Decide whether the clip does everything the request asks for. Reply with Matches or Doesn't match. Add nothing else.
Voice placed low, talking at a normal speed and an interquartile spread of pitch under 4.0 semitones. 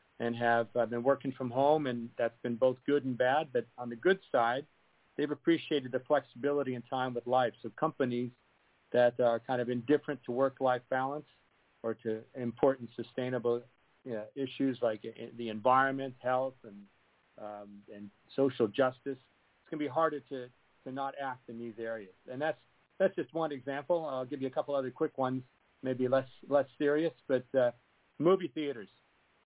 Matches